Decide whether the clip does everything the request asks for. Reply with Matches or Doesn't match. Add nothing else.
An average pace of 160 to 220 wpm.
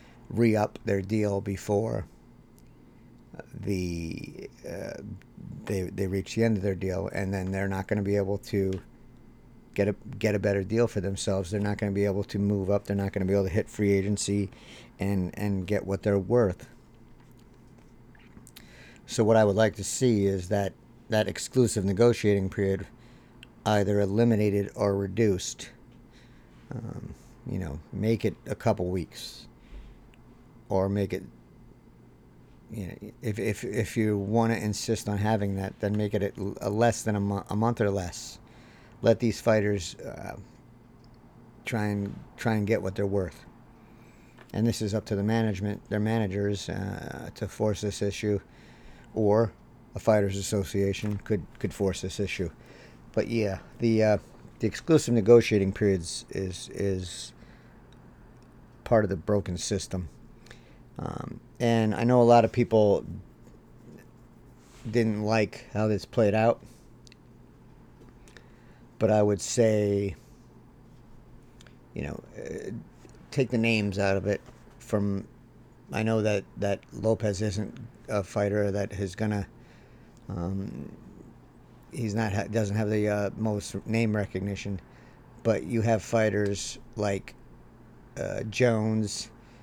Doesn't match